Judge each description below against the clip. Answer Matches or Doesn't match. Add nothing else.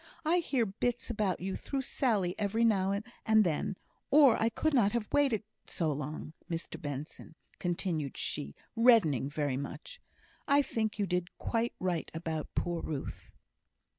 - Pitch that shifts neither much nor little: Doesn't match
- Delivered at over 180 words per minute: Doesn't match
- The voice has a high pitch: Matches